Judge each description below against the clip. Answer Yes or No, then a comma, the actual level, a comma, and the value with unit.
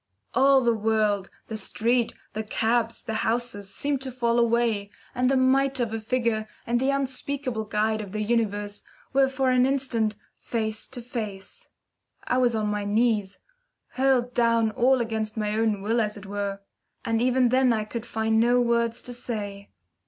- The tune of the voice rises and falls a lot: No, average, 2.7 semitones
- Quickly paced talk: No, average, 175 wpm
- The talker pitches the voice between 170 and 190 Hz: No, high, 230 Hz